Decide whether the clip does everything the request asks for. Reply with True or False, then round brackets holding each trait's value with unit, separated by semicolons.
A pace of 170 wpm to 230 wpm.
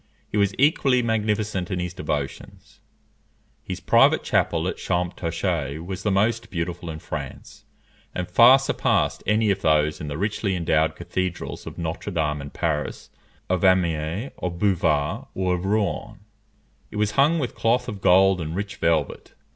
False (155 wpm)